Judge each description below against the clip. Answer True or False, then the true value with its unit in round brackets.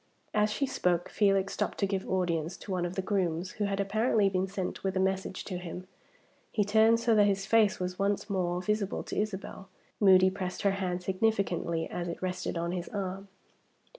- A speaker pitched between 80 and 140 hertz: False (190 Hz)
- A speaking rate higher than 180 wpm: True (195 wpm)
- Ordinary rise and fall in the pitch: False (2.1 semitones)